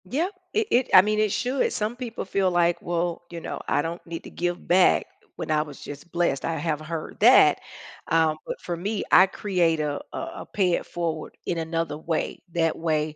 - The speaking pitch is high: No, medium, 170 Hz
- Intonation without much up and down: No, average, 3.2 semitones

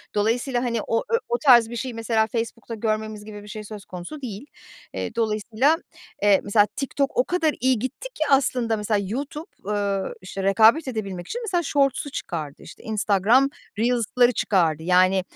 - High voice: Yes, high, 225 Hz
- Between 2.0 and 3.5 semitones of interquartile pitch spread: No, average, 4.1 semitones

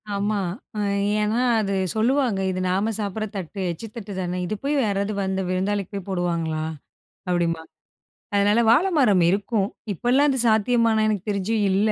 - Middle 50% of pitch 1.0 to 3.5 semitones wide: Yes, average, 3.0 semitones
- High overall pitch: Yes, high, 205 Hz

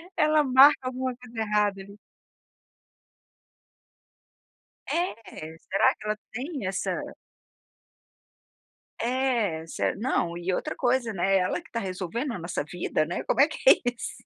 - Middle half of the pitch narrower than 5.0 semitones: No, wide, 5.5 semitones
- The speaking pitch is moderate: No, high, 220 Hz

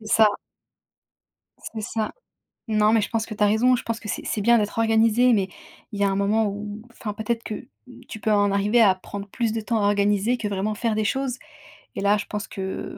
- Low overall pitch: No, high, 215 Hz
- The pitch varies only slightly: Yes, narrow, 1.8 semitones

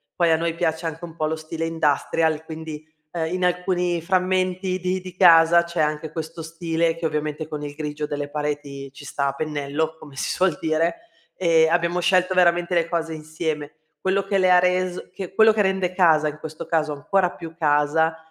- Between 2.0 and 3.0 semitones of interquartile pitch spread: Yes, narrow, 2.6 semitones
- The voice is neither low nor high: Yes, medium, 165 Hz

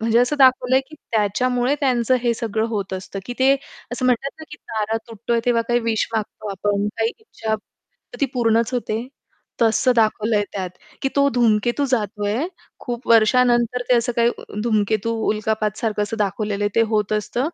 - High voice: Yes, high, 230 Hz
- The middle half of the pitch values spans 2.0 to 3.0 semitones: Yes, narrow, 2.6 semitones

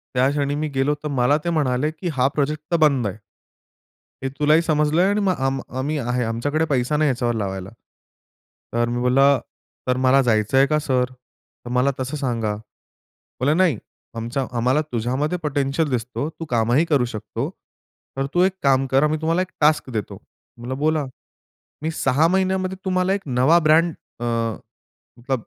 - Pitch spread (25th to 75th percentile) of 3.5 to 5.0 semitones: Yes, average, 3.8 semitones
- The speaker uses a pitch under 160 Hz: Yes, medium, 140 Hz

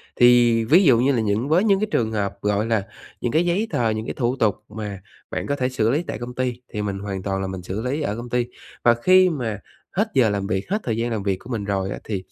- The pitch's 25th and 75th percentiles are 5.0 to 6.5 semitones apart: No, average, 4.1 semitones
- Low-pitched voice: Yes, low, 115 Hz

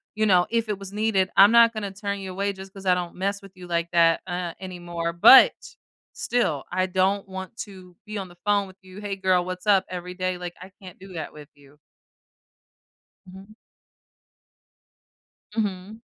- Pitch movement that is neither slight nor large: No, narrow, 2.0 semitones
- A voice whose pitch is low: No, high, 190 Hz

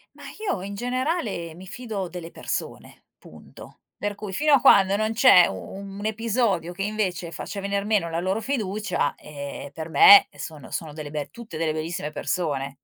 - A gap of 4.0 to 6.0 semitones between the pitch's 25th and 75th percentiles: Yes, average, 4.7 semitones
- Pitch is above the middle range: Yes, high, 195 Hz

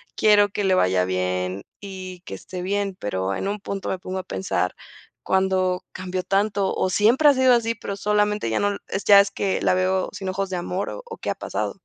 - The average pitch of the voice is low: No, high, 190 Hz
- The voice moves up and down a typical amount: No, narrow, 2.0 semitones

